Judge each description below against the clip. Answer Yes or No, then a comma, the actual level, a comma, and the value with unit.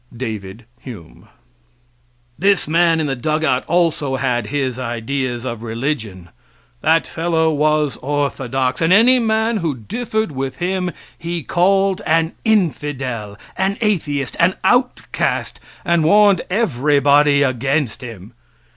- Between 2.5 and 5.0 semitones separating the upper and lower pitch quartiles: No, wide, 5.5 semitones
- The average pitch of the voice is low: No, medium, 150 Hz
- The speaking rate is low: Yes, slow, 120 wpm